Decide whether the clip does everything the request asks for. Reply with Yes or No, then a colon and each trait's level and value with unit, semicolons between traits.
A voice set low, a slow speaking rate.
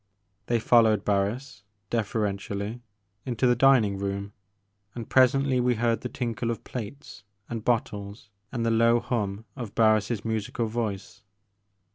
Yes: low, 115 Hz; slow, 130 wpm